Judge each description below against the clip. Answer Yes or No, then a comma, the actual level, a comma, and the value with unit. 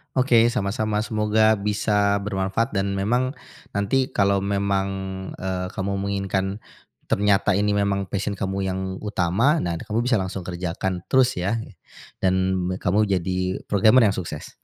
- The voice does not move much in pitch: Yes, narrow, 2.0 semitones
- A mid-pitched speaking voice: No, low, 100 Hz